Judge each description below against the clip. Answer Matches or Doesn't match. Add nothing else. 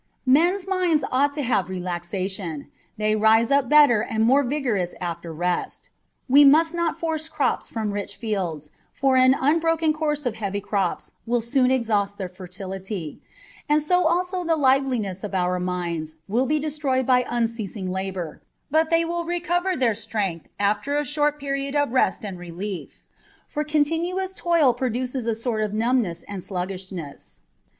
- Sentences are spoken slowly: Doesn't match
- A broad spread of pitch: Matches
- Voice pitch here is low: Doesn't match